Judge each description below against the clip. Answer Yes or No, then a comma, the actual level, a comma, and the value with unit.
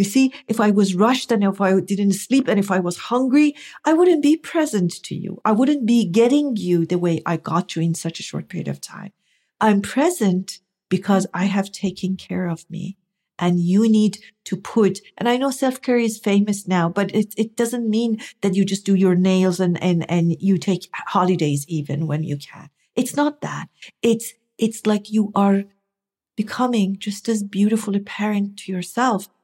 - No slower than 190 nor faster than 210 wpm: Yes, average, 200 wpm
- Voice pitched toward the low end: No, high, 200 Hz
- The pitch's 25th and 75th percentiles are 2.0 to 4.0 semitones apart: Yes, average, 3.5 semitones